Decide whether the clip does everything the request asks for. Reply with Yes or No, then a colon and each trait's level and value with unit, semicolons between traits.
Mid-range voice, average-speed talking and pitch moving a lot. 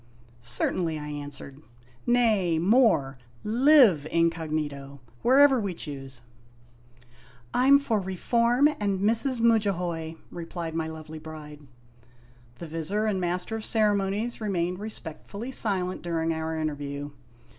No: medium, 170 Hz; slow, 120 wpm; wide, 6.1 semitones